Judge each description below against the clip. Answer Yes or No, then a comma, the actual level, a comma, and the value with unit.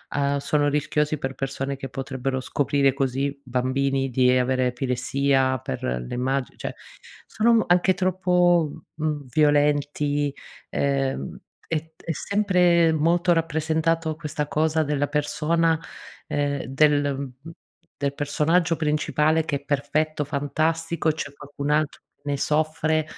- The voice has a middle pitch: Yes, medium, 145 Hz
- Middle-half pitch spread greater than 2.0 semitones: Yes, narrow, 2.6 semitones